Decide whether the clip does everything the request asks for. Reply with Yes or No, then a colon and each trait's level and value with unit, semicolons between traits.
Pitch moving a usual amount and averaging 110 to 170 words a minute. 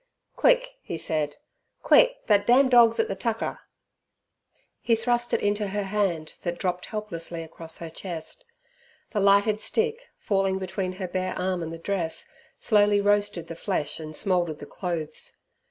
Yes: average, 3.9 semitones; average, 155 wpm